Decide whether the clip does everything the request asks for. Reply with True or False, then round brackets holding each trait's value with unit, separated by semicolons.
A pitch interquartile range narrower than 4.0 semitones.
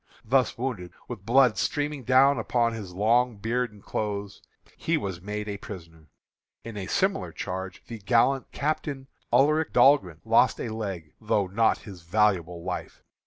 False (5.2 semitones)